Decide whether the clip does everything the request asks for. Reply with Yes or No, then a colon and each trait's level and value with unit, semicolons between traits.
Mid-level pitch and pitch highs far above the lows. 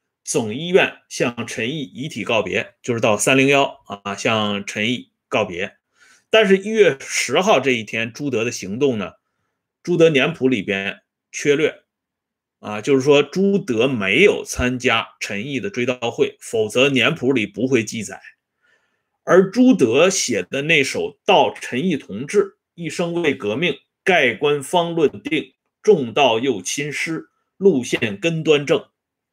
Yes: medium, 145 Hz; wide, 8.2 semitones